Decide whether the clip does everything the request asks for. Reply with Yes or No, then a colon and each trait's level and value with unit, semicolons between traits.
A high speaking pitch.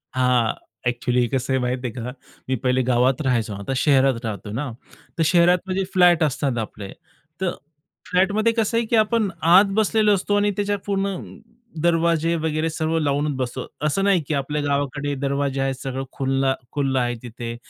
No: medium, 145 Hz